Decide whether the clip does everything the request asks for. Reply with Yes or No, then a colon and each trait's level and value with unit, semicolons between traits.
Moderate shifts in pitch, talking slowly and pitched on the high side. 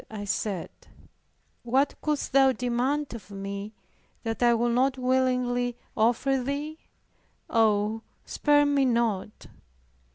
Yes: average, 3.3 semitones; slow, 110 wpm; high, 245 Hz